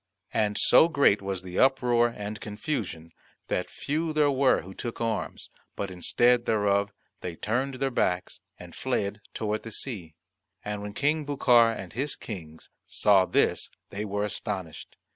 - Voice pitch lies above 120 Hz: No, low, 105 Hz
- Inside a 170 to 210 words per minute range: No, average, 155 wpm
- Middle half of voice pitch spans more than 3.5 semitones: Yes, average, 4.7 semitones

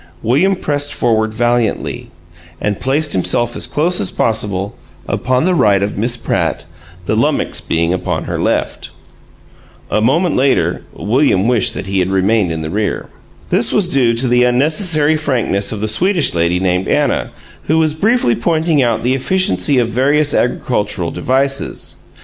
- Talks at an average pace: Yes, average, 160 wpm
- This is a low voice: Yes, low, 120 Hz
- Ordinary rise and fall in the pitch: No, wide, 6.3 semitones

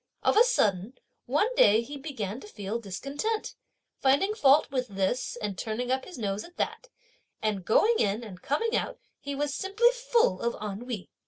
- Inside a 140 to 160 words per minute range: No, average, 175 wpm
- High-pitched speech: Yes, very high, 255 Hz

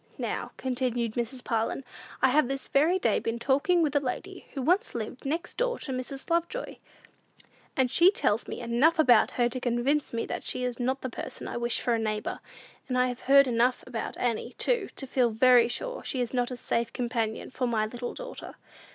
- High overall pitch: Yes, very high, 255 Hz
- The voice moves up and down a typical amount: Yes, average, 3.1 semitones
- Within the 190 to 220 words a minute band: Yes, fast, 205 wpm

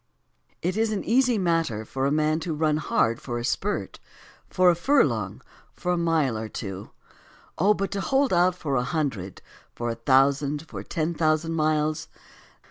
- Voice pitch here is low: No, medium, 155 Hz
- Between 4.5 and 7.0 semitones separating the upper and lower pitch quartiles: Yes, average, 5.0 semitones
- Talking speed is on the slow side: No, average, 175 wpm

